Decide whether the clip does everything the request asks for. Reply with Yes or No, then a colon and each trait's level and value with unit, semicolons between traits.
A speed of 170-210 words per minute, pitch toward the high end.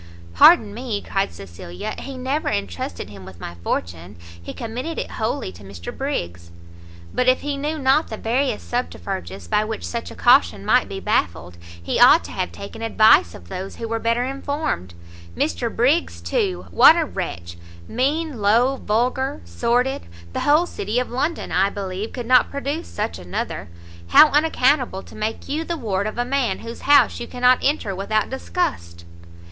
Yes: average, 175 wpm; high, 225 Hz